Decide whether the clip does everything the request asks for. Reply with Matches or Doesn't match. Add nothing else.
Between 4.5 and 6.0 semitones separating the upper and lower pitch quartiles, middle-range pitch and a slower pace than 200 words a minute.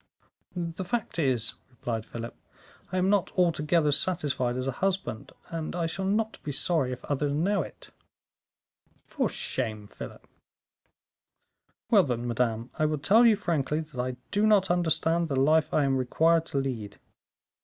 Matches